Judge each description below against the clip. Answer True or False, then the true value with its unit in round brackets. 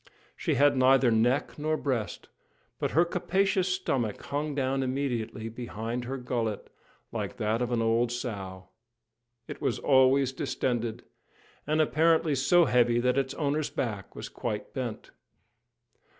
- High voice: False (130 Hz)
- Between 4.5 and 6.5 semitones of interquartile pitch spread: False (3.7 semitones)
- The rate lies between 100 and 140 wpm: True (135 wpm)